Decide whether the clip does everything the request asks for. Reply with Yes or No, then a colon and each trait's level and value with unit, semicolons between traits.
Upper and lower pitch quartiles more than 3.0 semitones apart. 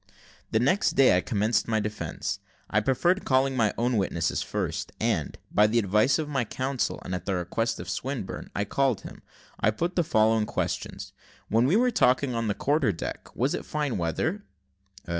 Yes: average, 4.7 semitones